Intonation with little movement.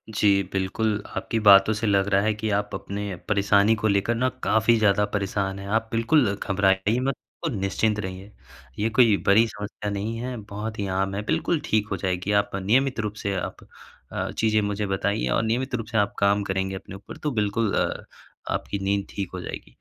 Yes: narrow, 2.0 semitones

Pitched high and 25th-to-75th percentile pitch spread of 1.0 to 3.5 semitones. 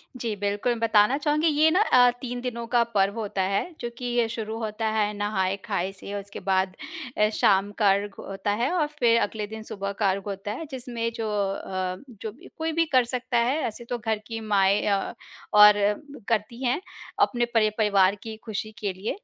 Yes: high, 215 Hz; average, 3.1 semitones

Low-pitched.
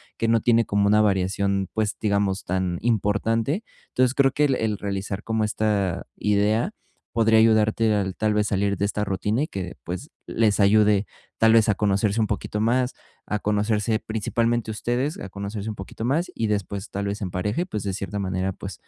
Yes: low, 105 Hz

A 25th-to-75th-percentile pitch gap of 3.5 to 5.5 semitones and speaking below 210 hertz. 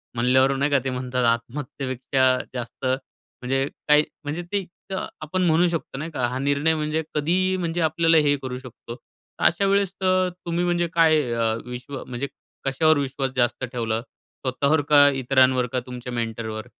Yes: average, 4.2 semitones; low, 135 Hz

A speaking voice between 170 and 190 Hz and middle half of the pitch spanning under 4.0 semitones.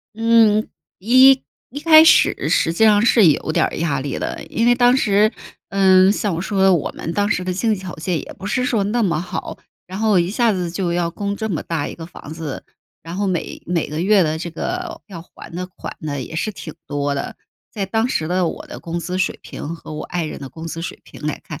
No: medium, 185 Hz; average, 4.6 semitones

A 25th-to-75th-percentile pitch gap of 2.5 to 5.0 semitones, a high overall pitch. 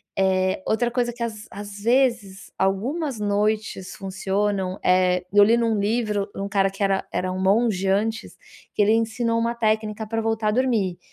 Yes: average, 2.9 semitones; high, 210 Hz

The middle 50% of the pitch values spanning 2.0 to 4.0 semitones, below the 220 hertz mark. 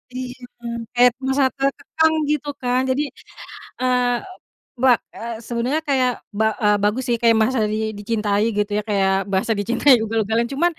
No: average, 3.1 semitones; high, 245 Hz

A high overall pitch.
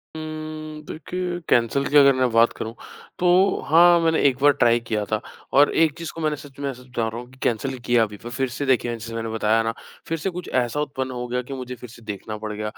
No: low, 130 Hz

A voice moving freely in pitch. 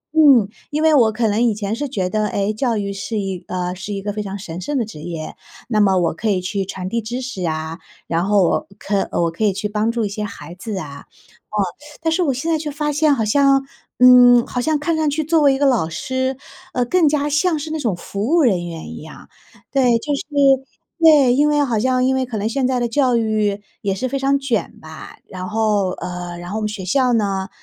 Yes: wide, 5.8 semitones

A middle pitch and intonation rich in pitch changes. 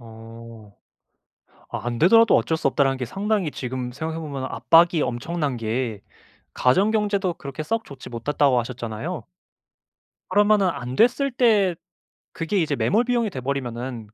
Yes: medium, 145 Hz; wide, 7.9 semitones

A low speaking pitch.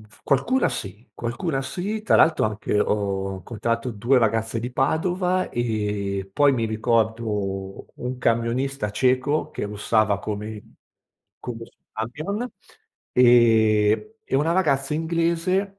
Yes: low, 115 Hz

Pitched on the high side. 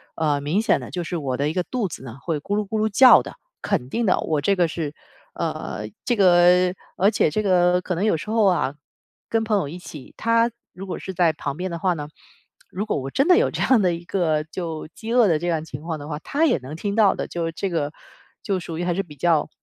No: medium, 175 Hz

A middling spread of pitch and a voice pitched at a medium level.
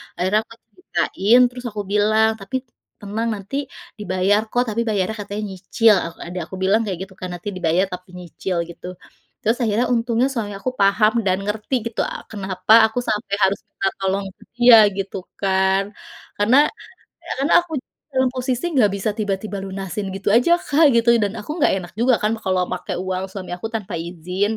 No: average, 3.0 semitones; high, 205 Hz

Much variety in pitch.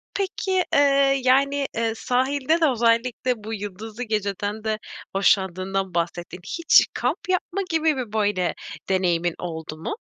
Yes: wide, 5.9 semitones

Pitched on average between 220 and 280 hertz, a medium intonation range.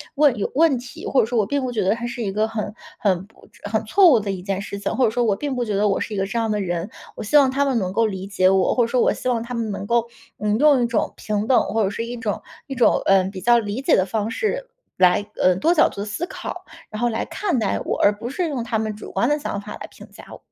Yes: high, 225 Hz; average, 3.7 semitones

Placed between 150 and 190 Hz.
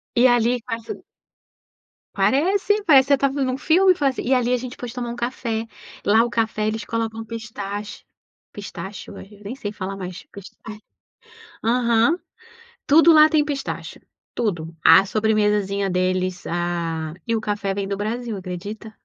No: high, 220 Hz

